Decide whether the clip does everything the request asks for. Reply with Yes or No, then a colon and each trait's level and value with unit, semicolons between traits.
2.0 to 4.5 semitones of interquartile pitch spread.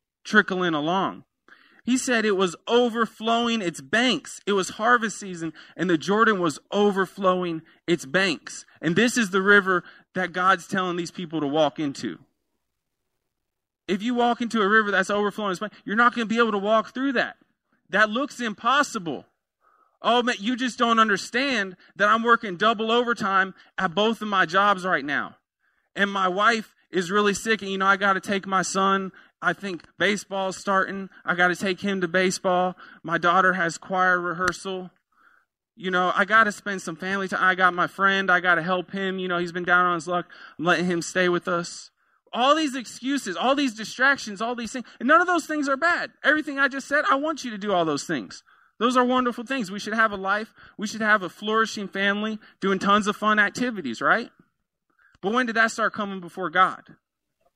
Yes: average, 3.9 semitones